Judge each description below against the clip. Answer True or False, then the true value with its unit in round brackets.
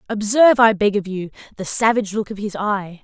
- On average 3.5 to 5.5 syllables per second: False (5.9 syllables/s)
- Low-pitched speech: False (205 Hz)